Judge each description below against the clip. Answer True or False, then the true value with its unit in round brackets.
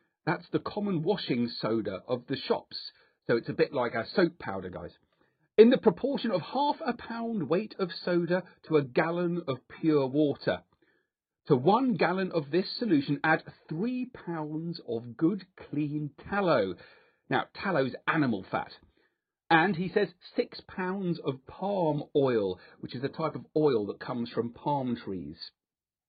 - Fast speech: False (160 wpm)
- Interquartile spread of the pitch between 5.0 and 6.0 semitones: True (5.4 semitones)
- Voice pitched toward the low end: False (160 Hz)